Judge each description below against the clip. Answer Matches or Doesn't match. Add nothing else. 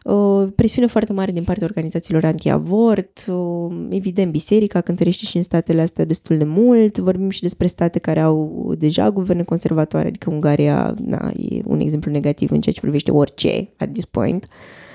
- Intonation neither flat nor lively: Matches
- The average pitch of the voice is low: Doesn't match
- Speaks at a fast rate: Matches